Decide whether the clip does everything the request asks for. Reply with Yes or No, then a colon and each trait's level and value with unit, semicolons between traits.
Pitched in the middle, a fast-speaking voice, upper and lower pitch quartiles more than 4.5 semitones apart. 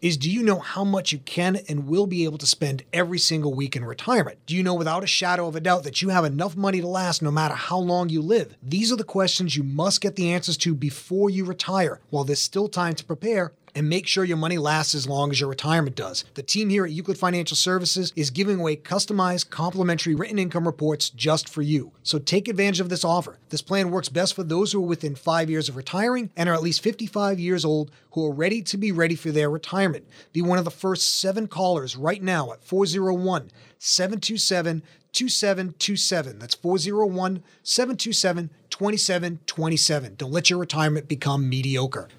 No: medium, 175 Hz; fast, 210 wpm; average, 3.7 semitones